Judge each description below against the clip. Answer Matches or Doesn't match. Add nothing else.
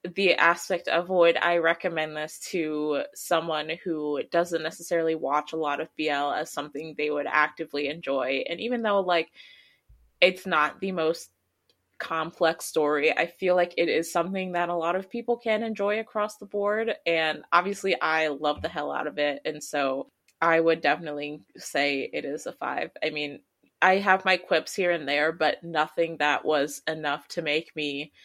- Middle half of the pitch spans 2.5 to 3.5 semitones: Matches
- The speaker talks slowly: Doesn't match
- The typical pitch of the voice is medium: Matches